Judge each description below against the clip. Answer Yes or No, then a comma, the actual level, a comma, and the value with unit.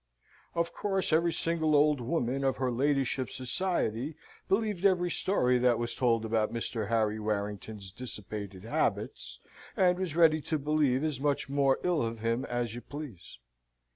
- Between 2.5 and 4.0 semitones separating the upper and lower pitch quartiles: No, wide, 5.5 semitones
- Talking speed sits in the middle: Yes, average, 155 wpm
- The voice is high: No, low, 130 Hz